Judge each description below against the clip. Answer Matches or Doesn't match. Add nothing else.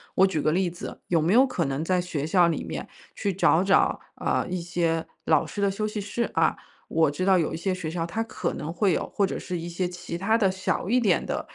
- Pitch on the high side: Doesn't match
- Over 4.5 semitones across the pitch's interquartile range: Doesn't match